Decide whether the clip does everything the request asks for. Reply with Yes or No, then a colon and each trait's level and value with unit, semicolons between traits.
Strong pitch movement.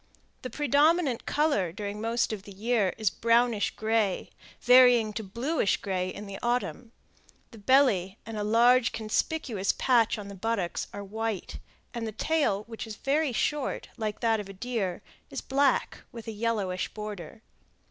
No: average, 3.4 semitones